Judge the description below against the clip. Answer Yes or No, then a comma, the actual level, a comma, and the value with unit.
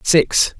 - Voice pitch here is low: No, medium, 155 Hz